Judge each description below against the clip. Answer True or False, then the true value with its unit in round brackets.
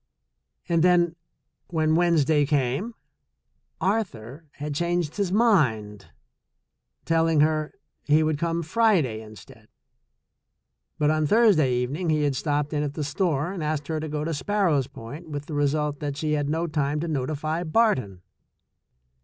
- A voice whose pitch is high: False (155 Hz)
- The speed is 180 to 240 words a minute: False (155 wpm)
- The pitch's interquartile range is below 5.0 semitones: True (2.9 semitones)